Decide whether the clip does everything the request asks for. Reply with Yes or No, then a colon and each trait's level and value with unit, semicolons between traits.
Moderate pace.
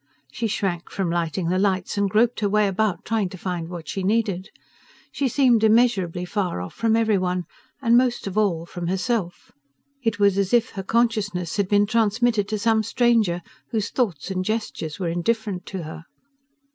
Yes: average, 185 wpm